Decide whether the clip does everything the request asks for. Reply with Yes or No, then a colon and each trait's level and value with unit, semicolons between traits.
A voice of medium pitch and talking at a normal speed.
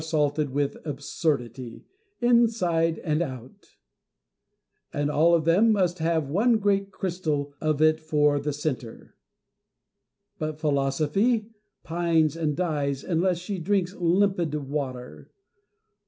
No: medium, 160 Hz; slow, 115 wpm